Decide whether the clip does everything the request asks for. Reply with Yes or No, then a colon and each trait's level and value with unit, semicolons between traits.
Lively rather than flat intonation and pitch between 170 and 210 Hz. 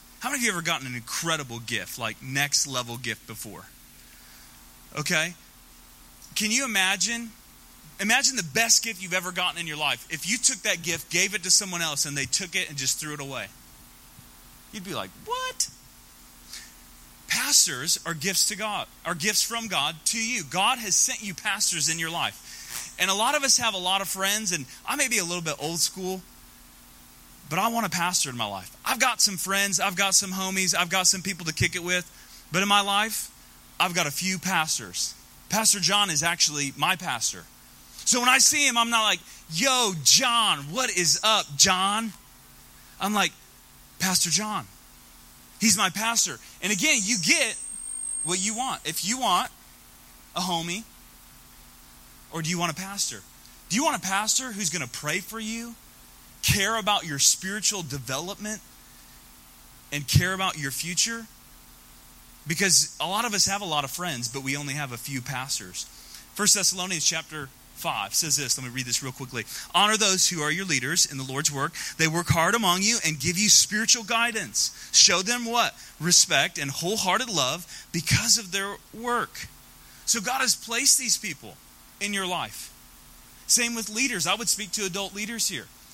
Yes: wide, 7.9 semitones; medium, 175 Hz